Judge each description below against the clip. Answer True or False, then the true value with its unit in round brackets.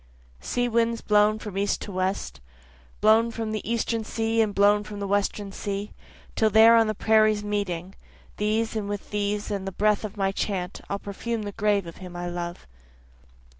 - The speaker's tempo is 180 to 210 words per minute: True (185 wpm)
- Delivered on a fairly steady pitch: True (1.8 semitones)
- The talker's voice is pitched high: True (210 Hz)